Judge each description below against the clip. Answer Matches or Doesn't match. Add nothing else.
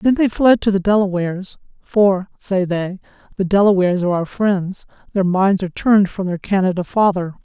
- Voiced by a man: Doesn't match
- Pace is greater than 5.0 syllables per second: Matches